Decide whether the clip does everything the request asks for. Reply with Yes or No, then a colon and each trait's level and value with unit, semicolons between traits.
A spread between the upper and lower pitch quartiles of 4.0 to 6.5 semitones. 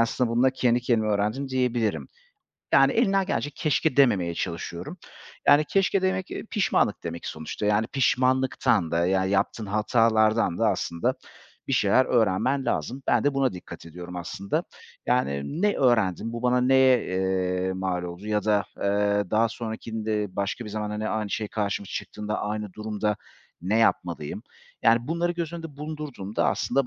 Yes: average, 5.0 semitones